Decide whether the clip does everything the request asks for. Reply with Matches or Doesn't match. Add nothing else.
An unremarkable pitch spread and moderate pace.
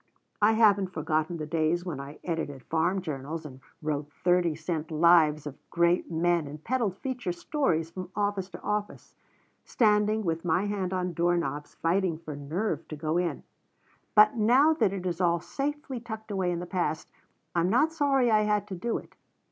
Matches